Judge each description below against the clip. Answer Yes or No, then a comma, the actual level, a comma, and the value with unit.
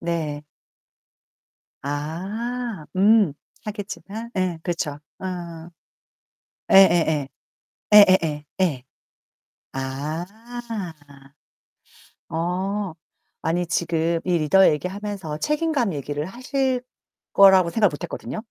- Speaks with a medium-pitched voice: Yes, medium, 175 Hz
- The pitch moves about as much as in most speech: Yes, average, 4.4 semitones